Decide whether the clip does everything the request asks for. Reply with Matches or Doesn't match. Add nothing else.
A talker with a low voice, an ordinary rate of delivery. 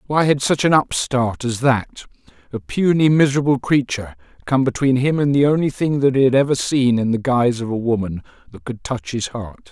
Doesn't match